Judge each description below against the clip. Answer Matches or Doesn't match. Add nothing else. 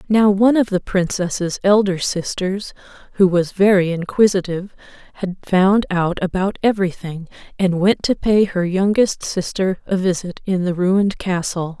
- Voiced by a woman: Matches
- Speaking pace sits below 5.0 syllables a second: Matches